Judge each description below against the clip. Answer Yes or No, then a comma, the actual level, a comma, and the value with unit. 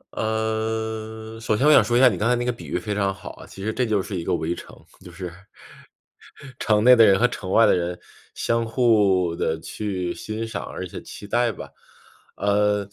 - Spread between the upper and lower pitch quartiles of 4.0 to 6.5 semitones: No, average, 2.8 semitones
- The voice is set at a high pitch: No, low, 110 Hz